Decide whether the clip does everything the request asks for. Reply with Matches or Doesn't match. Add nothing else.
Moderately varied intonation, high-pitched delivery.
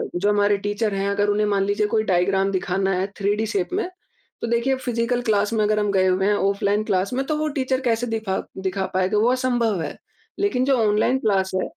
Matches